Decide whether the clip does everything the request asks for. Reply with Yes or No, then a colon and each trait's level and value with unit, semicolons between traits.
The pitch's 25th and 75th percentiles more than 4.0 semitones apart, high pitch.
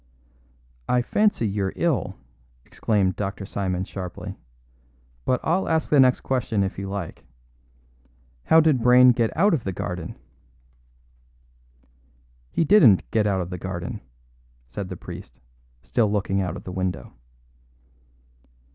No: average, 5.2 semitones; low, 100 Hz